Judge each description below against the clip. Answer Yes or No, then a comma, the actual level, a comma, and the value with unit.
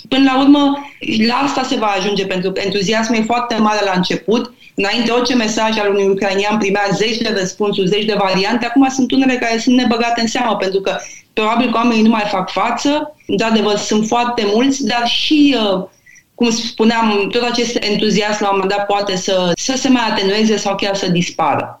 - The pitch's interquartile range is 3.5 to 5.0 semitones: No, average, 3.1 semitones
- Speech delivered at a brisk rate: Yes, fast, 195 wpm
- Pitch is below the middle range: No, high, 220 Hz